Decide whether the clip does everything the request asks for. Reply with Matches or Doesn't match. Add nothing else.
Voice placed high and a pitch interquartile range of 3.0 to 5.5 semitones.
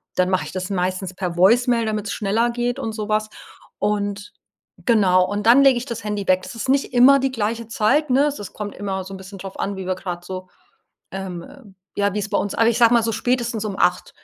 Matches